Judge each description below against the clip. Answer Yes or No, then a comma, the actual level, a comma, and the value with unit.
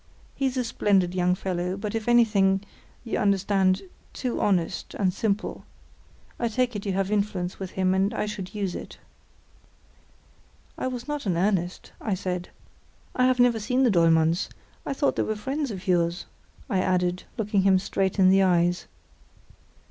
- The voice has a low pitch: No, high, 195 Hz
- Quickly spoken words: No, average, 160 wpm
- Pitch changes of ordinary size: Yes, average, 3.3 semitones